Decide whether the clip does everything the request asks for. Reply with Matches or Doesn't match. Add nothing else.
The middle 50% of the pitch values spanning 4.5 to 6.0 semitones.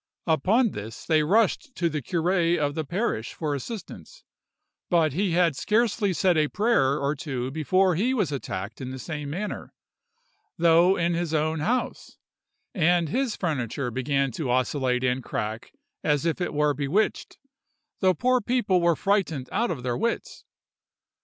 Matches